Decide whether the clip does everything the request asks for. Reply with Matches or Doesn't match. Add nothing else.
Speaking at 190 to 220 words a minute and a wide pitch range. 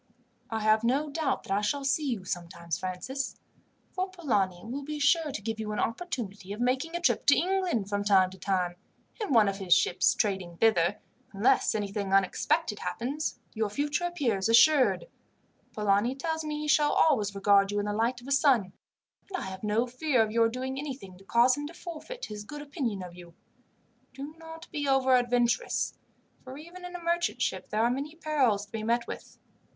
Matches